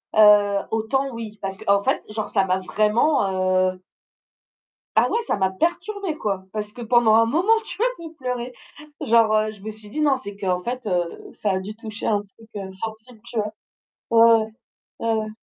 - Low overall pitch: No, high, 215 Hz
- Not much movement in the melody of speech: No, average, 3.3 semitones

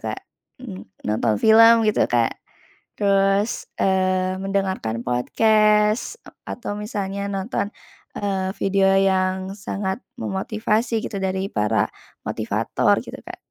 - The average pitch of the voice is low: No, high, 195 Hz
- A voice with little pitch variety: Yes, narrow, 2.1 semitones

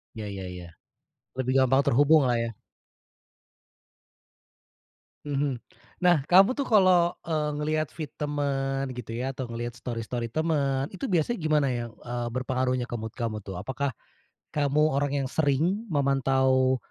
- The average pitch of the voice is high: No, low, 135 Hz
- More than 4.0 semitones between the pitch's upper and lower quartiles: No, average, 3.6 semitones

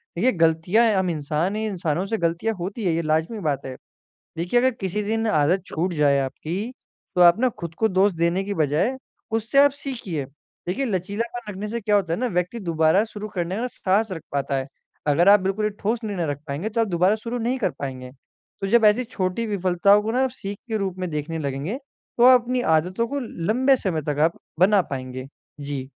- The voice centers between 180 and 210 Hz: Yes, high, 190 Hz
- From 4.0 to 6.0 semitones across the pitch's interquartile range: Yes, average, 5.3 semitones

